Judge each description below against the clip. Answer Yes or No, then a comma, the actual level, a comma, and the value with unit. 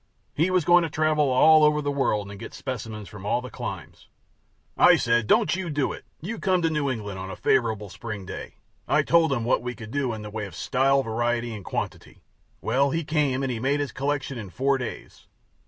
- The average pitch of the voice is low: Yes, low, 130 Hz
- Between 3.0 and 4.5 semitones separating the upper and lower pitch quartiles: No, average, 5.1 semitones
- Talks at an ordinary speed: No, fast, 220 wpm